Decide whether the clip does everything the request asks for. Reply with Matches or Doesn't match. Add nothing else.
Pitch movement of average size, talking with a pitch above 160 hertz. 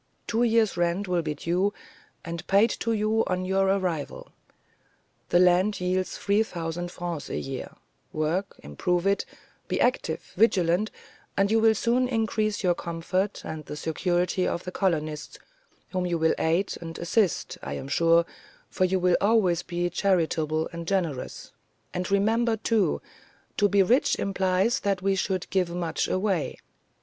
Matches